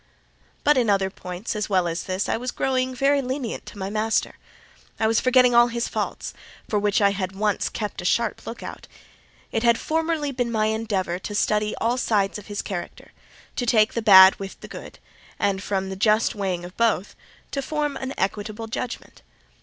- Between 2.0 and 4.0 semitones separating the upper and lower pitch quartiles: Yes, average, 3.7 semitones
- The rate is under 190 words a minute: No, average, 195 wpm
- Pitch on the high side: Yes, high, 215 Hz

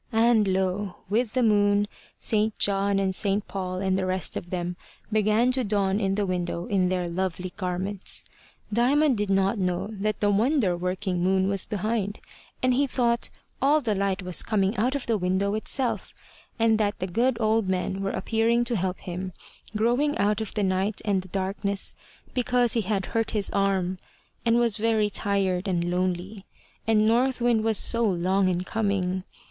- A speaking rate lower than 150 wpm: No, average, 180 wpm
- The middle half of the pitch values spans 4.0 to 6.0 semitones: No, average, 3.1 semitones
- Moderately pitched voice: No, high, 200 Hz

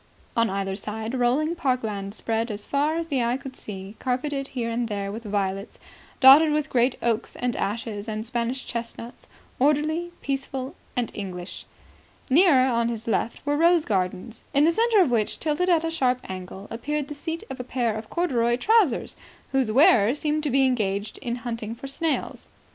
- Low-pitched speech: No, high, 245 Hz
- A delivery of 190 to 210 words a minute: No, average, 180 wpm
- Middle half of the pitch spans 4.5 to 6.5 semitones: Yes, average, 4.9 semitones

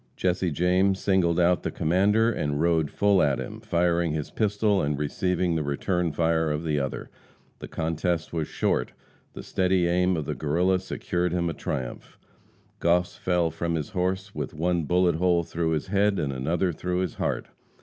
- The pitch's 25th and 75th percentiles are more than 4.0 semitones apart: No, narrow, 2.5 semitones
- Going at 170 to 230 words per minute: Yes, average, 180 wpm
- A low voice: Yes, very low, 85 Hz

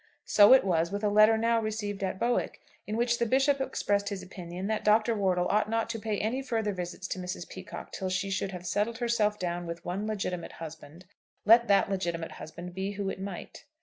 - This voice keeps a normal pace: No, fast, 215 wpm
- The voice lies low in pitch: No, high, 200 Hz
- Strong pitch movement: No, average, 3.4 semitones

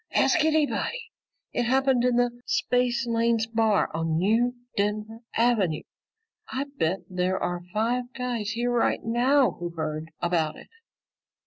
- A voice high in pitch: Yes, high, 230 Hz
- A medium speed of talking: No, slow, 130 wpm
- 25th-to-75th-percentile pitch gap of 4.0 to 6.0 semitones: Yes, average, 5.1 semitones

